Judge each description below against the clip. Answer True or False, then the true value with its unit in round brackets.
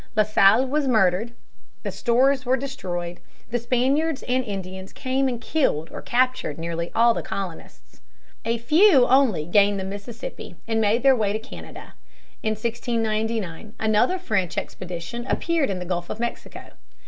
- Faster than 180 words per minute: False (155 wpm)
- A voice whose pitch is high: True (225 Hz)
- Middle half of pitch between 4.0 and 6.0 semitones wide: True (5.2 semitones)